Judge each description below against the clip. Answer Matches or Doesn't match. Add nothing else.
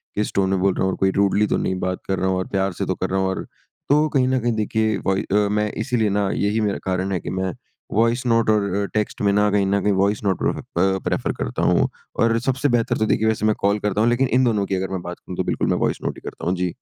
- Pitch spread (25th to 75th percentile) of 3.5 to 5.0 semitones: Doesn't match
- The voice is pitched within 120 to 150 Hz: Doesn't match